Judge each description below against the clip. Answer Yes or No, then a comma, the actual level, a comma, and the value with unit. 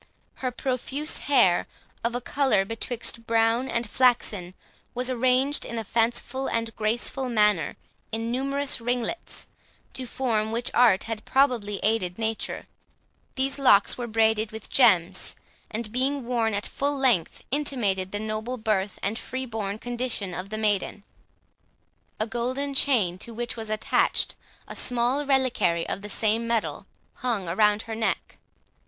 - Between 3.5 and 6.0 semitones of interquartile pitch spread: No, average, 3.1 semitones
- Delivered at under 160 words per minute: Yes, average, 145 wpm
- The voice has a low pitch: No, high, 230 Hz